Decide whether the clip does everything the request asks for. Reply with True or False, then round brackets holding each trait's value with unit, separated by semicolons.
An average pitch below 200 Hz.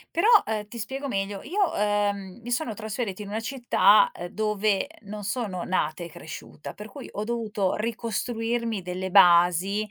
False (210 Hz)